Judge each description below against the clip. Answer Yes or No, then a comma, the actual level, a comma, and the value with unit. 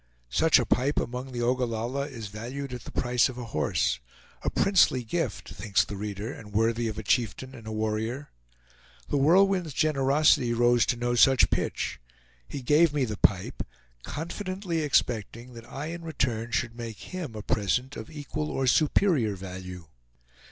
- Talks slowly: No, average, 165 wpm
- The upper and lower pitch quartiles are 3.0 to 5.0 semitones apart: Yes, average, 4.6 semitones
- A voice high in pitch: No, low, 125 Hz